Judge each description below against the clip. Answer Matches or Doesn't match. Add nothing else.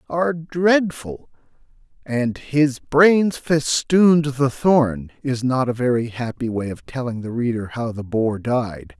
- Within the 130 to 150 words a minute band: Matches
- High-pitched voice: Doesn't match